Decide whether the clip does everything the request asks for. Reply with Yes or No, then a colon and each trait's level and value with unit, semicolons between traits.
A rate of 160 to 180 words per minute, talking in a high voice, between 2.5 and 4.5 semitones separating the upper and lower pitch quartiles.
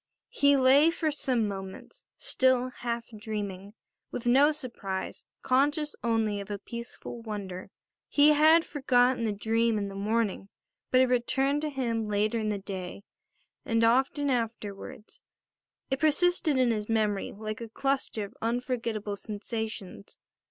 No: average, 140 wpm; high, 230 Hz; average, 4.1 semitones